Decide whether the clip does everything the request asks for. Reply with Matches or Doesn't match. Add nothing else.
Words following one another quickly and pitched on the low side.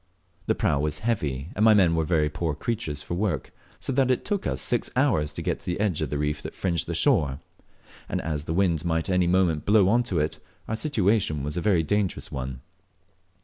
Matches